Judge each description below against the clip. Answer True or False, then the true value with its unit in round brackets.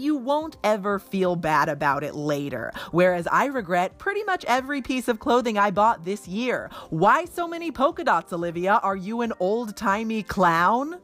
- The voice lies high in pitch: True (215 Hz)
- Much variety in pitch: True (7.0 semitones)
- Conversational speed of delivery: True (180 wpm)